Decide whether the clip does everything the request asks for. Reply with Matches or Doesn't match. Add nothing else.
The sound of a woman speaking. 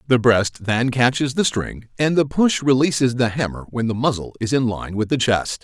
Doesn't match